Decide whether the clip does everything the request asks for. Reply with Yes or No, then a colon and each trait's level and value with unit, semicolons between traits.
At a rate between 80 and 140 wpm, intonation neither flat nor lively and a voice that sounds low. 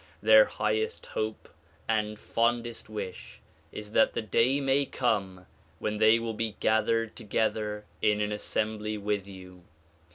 No: slow, 135 wpm; narrow, 1.7 semitones; low, 110 Hz